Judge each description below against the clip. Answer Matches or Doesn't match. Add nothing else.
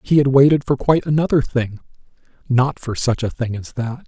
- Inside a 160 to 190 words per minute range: Doesn't match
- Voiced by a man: Matches